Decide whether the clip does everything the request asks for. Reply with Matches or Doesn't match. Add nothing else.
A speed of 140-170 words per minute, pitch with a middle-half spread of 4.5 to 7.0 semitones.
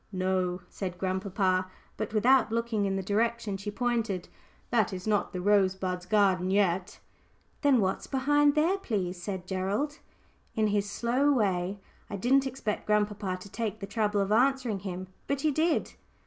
Doesn't match